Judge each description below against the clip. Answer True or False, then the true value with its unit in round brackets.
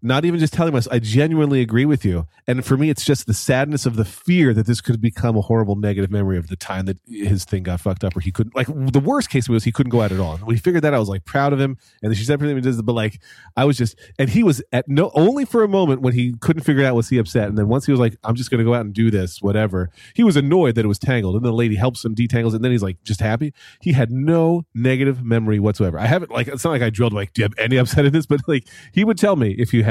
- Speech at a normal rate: False (310 wpm)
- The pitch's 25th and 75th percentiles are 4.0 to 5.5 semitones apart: True (4.4 semitones)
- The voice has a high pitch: False (120 Hz)